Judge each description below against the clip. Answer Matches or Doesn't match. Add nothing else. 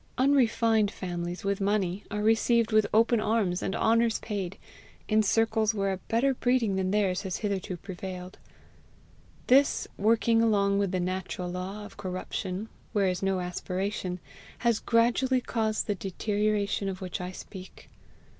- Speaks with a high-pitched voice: Matches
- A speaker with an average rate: Matches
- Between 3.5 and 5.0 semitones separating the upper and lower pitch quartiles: Doesn't match